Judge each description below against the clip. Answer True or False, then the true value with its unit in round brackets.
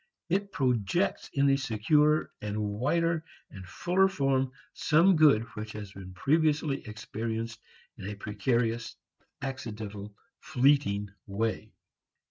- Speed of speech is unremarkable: False (105 wpm)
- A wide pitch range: True (6.1 semitones)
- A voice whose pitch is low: True (115 Hz)